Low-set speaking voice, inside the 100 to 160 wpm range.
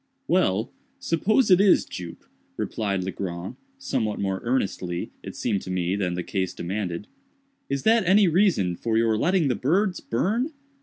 Yes: low, 110 Hz; average, 155 wpm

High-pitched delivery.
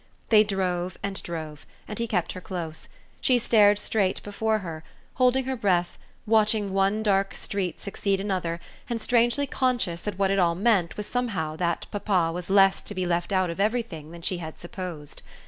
Yes: high, 195 Hz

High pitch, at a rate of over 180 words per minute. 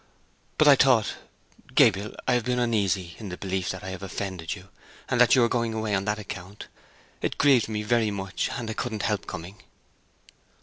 No: low, 105 Hz; average, 190 wpm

